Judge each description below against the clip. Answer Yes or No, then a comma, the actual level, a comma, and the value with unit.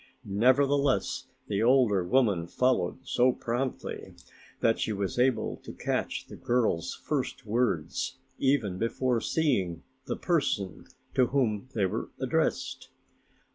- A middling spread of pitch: Yes, average, 4.4 semitones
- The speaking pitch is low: Yes, low, 120 Hz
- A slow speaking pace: Yes, slow, 120 wpm